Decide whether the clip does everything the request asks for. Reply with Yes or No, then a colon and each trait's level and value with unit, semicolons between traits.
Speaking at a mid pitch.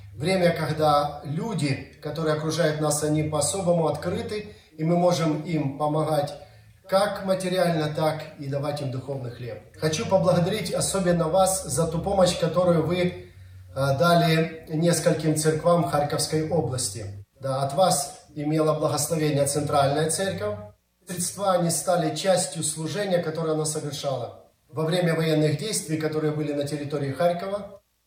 Yes: medium, 155 Hz